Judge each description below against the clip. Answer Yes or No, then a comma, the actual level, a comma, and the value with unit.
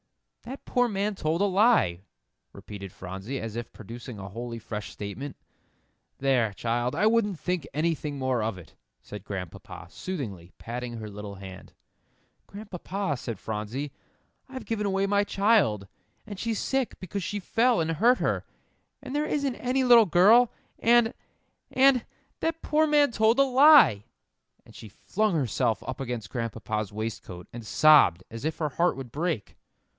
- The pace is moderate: Yes, average, 155 wpm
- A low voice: No, medium, 150 Hz